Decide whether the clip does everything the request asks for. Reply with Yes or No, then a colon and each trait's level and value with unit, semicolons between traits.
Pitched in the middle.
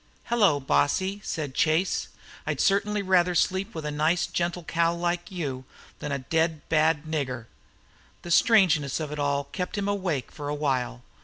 Yes: medium, 160 Hz